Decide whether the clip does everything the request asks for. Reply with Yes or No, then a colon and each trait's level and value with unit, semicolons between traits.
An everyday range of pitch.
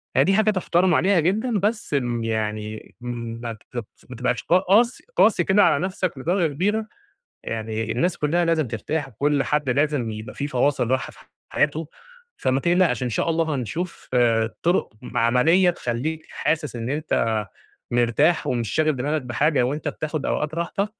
No: wide, 6.2 semitones